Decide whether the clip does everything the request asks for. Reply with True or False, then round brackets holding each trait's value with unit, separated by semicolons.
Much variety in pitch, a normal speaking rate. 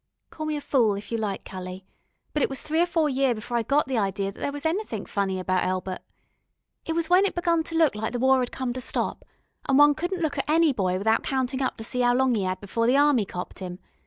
False (6.6 semitones; 270 wpm)